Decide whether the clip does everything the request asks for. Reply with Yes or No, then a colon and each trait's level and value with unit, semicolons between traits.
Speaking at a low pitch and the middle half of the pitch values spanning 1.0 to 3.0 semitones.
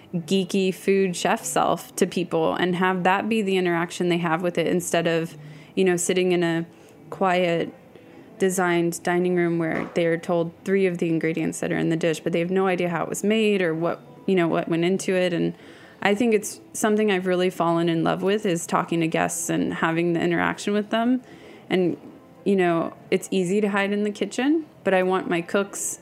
No: medium, 180 Hz; narrow, 2.5 semitones